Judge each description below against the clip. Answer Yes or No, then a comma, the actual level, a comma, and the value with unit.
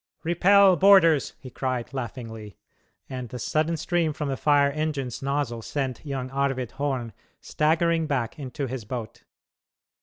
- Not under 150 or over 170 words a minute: No, average, 140 wpm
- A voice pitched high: No, medium, 140 Hz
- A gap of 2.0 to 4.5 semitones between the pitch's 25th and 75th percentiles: Yes, average, 3.7 semitones